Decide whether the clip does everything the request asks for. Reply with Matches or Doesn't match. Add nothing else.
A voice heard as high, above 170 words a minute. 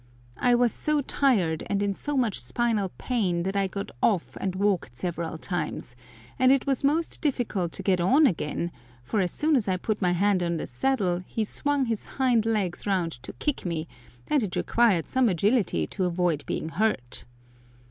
Matches